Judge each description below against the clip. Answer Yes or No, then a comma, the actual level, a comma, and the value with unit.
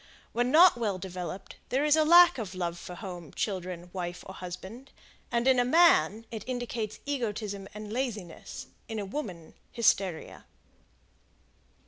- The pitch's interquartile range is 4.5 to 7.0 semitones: Yes, average, 5.2 semitones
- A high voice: Yes, high, 210 Hz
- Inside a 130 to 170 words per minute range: Yes, average, 145 wpm